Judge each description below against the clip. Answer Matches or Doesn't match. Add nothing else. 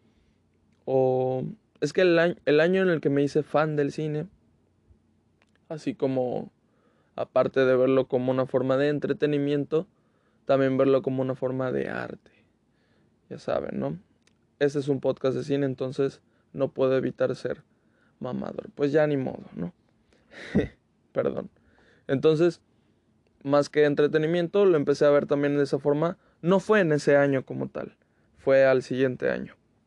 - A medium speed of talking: Matches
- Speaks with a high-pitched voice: Doesn't match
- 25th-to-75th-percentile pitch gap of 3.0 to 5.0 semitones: Doesn't match